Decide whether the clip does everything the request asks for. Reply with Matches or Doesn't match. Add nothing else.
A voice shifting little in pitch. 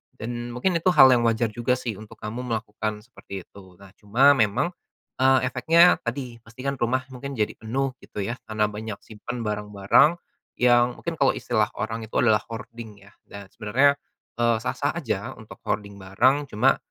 Doesn't match